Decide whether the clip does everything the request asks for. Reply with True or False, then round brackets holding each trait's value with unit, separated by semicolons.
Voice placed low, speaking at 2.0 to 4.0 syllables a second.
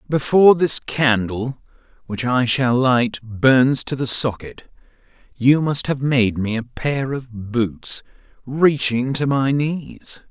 True (130 Hz; 3.4 syllables/s)